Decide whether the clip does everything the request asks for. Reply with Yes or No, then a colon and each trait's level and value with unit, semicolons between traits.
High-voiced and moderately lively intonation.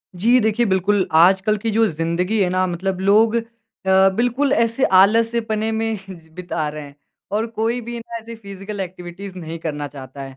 Yes: high, 200 Hz; average, 4.2 semitones